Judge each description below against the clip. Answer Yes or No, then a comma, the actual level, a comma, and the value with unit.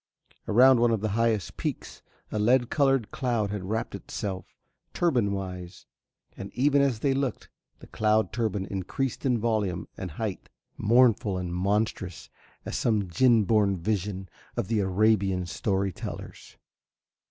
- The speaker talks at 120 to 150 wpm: Yes, average, 140 wpm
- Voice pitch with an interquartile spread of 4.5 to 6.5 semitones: No, average, 3.6 semitones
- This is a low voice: Yes, low, 105 Hz